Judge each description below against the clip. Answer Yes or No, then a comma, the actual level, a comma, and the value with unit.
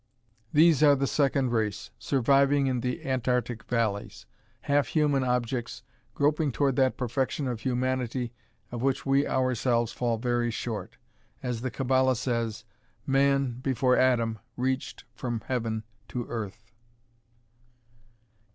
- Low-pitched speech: Yes, low, 125 Hz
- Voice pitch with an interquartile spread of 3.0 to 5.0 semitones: No, narrow, 2.4 semitones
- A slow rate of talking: Yes, slow, 125 wpm